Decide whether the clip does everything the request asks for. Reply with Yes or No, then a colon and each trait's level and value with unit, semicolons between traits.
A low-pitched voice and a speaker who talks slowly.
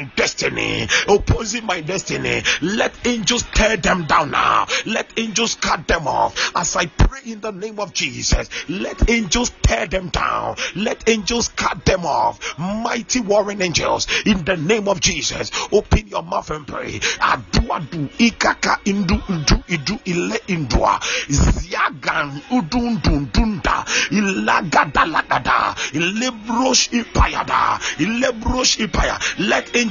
No: high, 215 Hz; slow, 95 wpm